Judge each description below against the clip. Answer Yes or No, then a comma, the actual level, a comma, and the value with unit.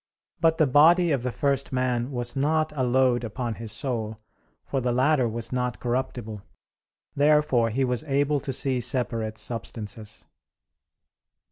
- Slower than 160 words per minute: Yes, average, 145 wpm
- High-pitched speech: No, low, 125 Hz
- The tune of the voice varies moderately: Yes, average, 3.1 semitones